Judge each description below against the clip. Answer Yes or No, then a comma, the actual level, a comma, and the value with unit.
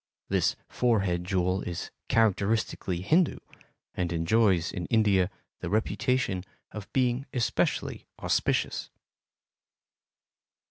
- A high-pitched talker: No, low, 100 Hz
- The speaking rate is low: Yes, slow, 90 wpm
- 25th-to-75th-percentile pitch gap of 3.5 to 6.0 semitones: Yes, average, 4.1 semitones